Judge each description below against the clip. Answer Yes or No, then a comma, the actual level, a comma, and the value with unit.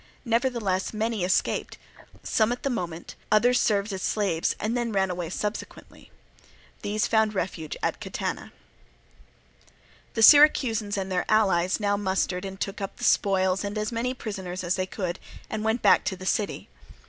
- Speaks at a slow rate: No, average, 160 wpm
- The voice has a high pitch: Yes, high, 205 Hz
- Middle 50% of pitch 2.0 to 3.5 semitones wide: Yes, average, 2.9 semitones